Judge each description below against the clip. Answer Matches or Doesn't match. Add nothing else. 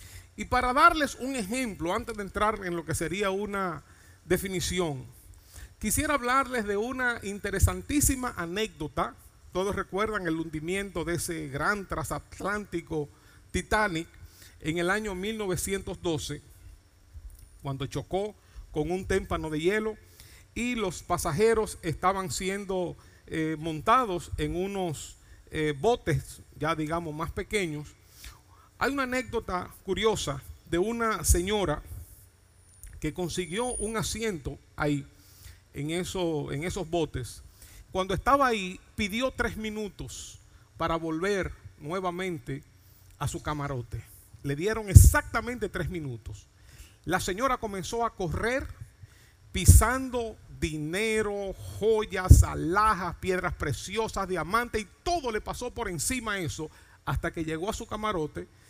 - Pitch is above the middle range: Doesn't match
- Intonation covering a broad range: Matches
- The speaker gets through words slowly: Matches